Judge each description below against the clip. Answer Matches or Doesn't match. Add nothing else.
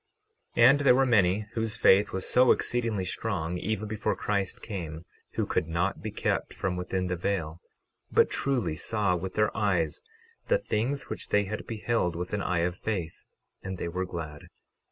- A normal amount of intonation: Matches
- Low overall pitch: Matches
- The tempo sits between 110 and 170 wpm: Doesn't match